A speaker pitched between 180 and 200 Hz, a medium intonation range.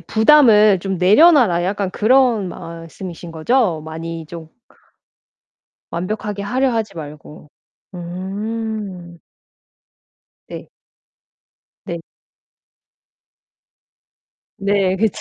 Yes: high, 190 Hz; average, 4.3 semitones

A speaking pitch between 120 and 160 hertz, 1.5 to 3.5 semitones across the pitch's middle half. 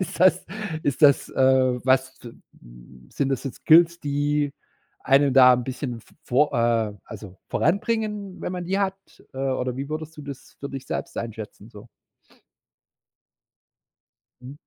No: low, 135 Hz; average, 3.9 semitones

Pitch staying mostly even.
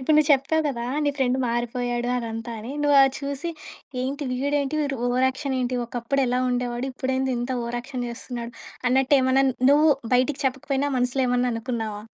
Yes: narrow, 2.2 semitones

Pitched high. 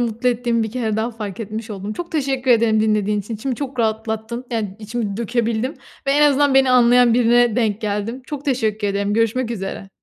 Yes: high, 230 Hz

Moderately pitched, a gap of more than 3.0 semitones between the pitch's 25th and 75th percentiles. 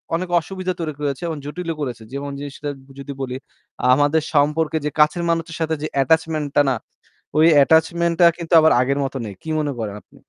No: medium, 155 Hz; narrow, 2.4 semitones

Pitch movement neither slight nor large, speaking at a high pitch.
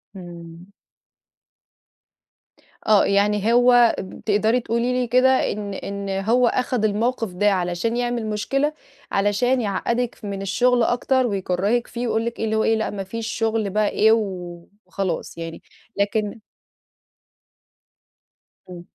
Yes: average, 3.4 semitones; high, 215 Hz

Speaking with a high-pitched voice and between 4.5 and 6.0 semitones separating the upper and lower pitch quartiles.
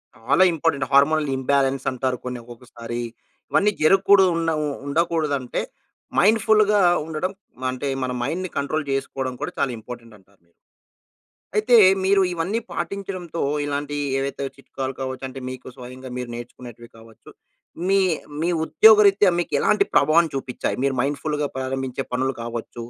No: medium, 140 Hz; average, 5.2 semitones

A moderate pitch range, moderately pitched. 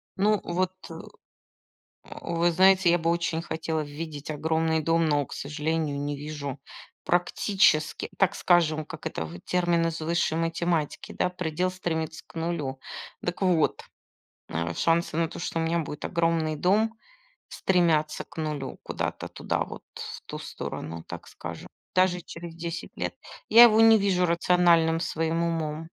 No: narrow, 2.1 semitones; medium, 165 Hz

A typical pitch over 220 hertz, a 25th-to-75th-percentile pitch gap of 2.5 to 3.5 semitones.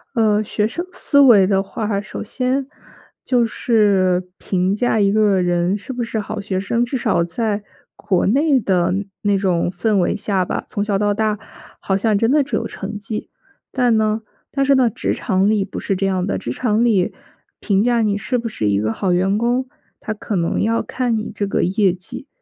No: high, 210 Hz; average, 3.2 semitones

